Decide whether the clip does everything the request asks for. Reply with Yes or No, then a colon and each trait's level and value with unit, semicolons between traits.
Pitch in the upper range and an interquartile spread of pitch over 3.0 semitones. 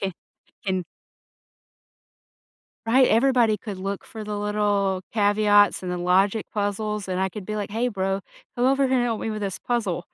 No: high, 205 Hz; narrow, 2.5 semitones